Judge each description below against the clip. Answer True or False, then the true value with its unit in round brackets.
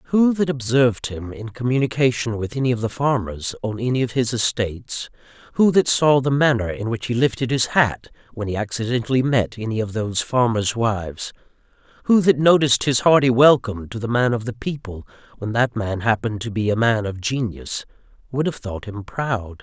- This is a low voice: True (120 Hz)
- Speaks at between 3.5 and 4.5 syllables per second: False (5.4 syllables/s)